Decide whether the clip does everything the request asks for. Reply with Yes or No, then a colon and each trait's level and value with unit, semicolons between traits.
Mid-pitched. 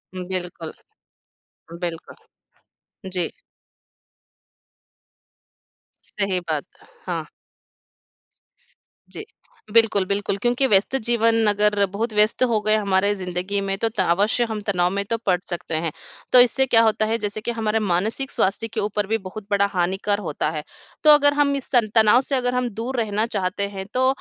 No: high, 210 Hz